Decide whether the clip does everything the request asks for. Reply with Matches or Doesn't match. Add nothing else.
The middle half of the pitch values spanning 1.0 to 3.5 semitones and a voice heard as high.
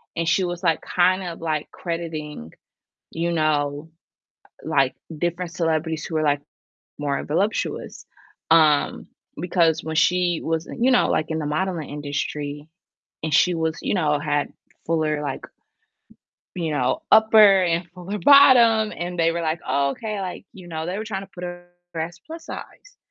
Doesn't match